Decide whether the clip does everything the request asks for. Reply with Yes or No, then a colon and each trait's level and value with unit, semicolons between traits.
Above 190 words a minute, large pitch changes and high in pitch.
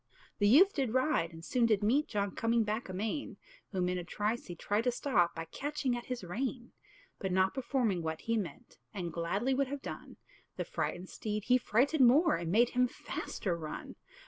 Yes: average, 200 wpm; wide, 5.8 semitones; high, 220 Hz